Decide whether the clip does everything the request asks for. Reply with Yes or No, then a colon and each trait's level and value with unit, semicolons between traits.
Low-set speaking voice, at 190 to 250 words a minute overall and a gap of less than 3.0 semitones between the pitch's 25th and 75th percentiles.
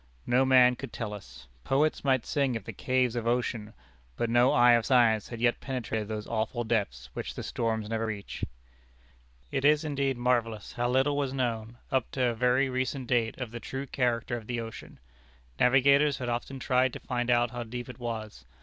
Yes: low, 120 Hz; average, 195 wpm; narrow, 2.4 semitones